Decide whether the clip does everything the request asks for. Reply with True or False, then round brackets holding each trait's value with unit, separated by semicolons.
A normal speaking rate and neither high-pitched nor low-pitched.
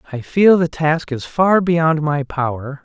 True (190 wpm; 155 Hz)